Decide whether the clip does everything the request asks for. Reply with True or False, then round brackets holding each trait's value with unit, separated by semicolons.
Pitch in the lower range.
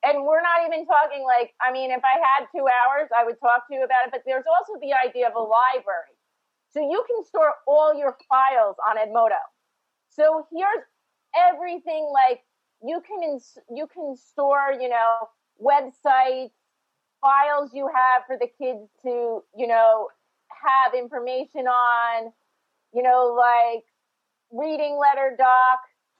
False (260 Hz)